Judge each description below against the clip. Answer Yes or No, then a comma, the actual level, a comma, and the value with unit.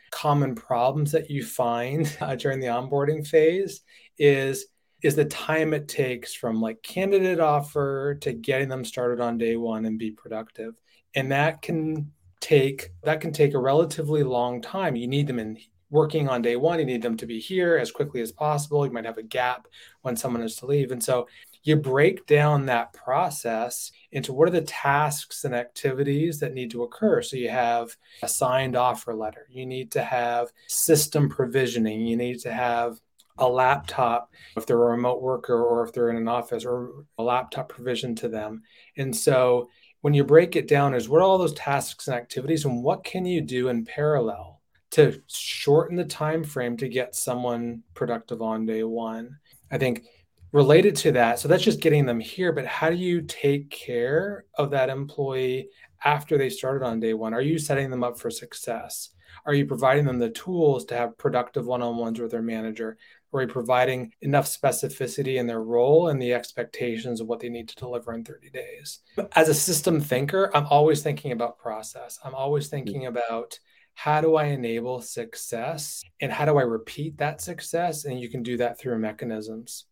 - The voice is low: Yes, low, 130 Hz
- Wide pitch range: No, average, 4.0 semitones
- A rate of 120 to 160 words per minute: No, average, 195 wpm